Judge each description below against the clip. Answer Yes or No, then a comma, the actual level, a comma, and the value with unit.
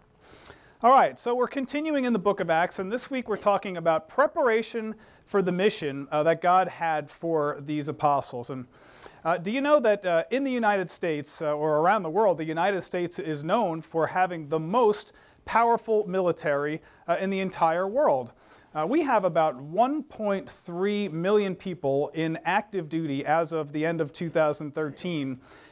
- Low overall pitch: No, medium, 175 Hz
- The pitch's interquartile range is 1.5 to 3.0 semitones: No, average, 5.1 semitones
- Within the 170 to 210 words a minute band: Yes, average, 175 wpm